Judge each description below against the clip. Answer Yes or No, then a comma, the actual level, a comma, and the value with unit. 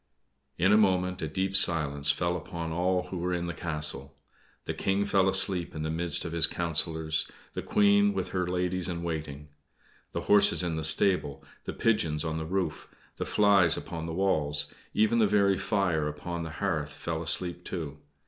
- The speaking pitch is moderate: No, very low, 85 Hz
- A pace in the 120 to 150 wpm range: No, average, 185 wpm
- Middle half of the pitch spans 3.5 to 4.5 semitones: No, average, 3.1 semitones